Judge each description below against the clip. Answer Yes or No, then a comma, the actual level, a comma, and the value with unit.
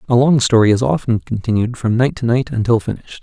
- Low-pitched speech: Yes, low, 120 Hz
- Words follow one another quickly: Yes, fast, 225 wpm